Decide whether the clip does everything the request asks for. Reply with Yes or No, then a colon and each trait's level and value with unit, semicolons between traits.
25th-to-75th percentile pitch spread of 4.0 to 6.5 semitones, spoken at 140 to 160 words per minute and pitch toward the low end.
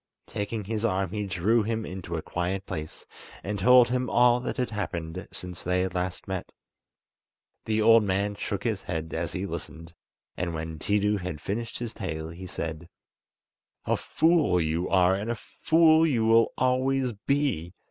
No: average, 4.6 semitones; average, 170 wpm; low, 100 Hz